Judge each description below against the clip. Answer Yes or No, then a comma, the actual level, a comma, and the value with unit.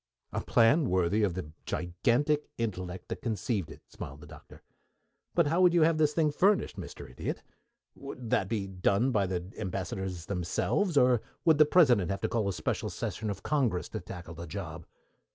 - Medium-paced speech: Yes, average, 185 wpm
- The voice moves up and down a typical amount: No, wide, 8.1 semitones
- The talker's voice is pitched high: No, low, 105 Hz